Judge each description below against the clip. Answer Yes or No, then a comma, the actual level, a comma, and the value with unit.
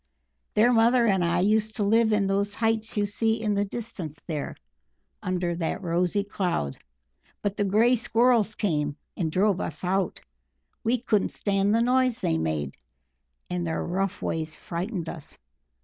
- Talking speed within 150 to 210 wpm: Yes, average, 160 wpm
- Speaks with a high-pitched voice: Yes, high, 200 Hz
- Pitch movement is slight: No, average, 4.3 semitones